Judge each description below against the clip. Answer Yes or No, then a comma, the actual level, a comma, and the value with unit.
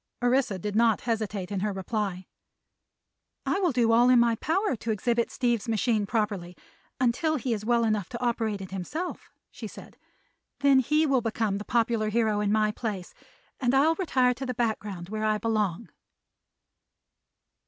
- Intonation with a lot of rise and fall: No, average, 3.0 semitones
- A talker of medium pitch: No, high, 225 Hz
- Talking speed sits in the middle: Yes, average, 165 wpm